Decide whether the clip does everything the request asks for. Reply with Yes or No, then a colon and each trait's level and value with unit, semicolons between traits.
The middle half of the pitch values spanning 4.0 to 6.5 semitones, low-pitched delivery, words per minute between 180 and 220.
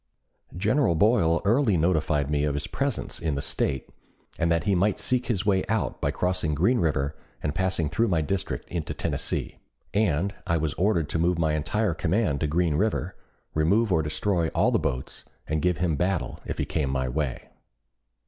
Yes: average, 4.4 semitones; very low, 85 Hz; average, 185 wpm